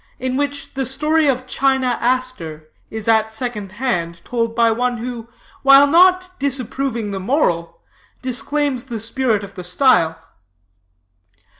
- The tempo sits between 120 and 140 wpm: Yes, slow, 135 wpm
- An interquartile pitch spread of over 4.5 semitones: No, average, 3.7 semitones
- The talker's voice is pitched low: No, very high, 250 Hz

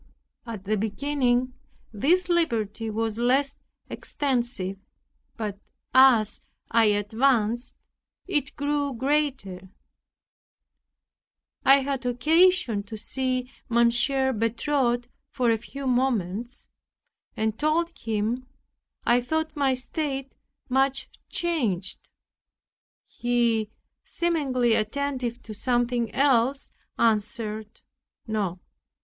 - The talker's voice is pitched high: Yes, high, 245 Hz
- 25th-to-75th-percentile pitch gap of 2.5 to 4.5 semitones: Yes, average, 3.8 semitones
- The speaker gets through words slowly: Yes, slow, 90 wpm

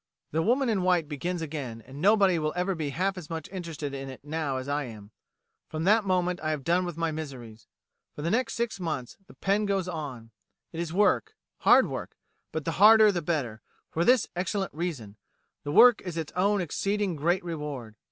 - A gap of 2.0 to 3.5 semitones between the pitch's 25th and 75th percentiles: No, average, 4.8 semitones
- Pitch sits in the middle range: Yes, medium, 165 Hz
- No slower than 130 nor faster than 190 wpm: No, average, 200 wpm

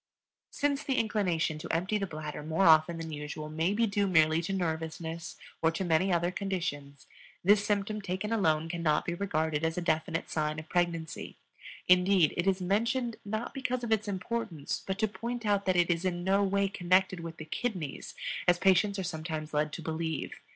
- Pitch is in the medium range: Yes, medium, 175 Hz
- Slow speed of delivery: No, average, 190 wpm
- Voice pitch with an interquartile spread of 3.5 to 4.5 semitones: Yes, average, 3.8 semitones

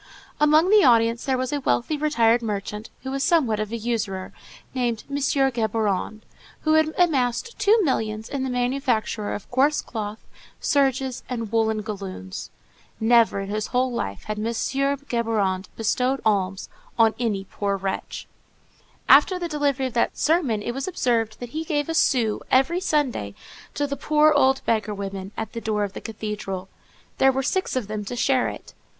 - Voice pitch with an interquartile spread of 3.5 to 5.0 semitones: Yes, average, 4.4 semitones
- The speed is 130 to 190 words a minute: Yes, average, 170 wpm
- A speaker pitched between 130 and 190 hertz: No, high, 240 Hz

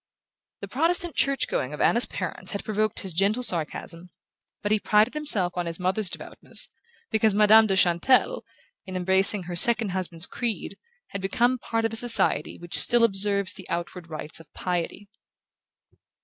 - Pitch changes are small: No, average, 4.1 semitones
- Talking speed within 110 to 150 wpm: No, average, 165 wpm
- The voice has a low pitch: No, high, 200 Hz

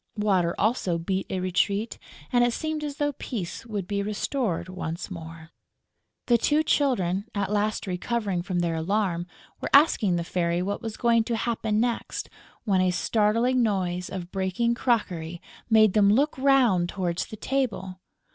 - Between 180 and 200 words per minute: No, average, 160 wpm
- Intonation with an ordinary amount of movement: Yes, average, 4.6 semitones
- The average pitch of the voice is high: Yes, high, 200 Hz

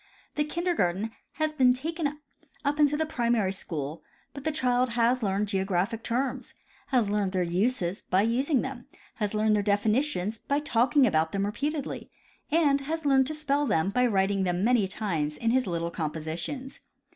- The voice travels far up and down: Yes, wide, 6.4 semitones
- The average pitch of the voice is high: Yes, high, 230 Hz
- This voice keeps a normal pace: Yes, average, 170 wpm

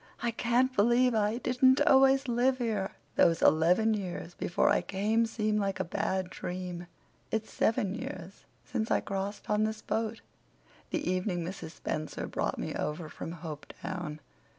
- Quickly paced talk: No, average, 150 wpm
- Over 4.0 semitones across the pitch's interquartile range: Yes, average, 4.7 semitones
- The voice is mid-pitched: No, high, 210 Hz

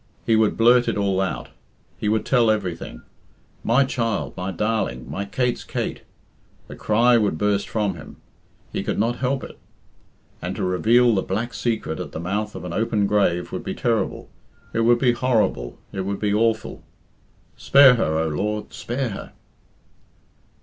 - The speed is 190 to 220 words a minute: No, average, 170 wpm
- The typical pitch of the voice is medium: No, low, 110 Hz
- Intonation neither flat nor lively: Yes, average, 3.6 semitones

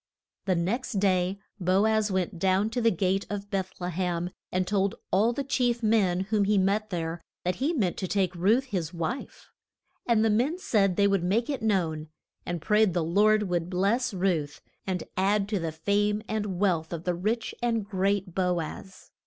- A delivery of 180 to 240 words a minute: Yes, average, 195 wpm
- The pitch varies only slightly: No, average, 3.2 semitones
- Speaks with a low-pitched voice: No, high, 195 Hz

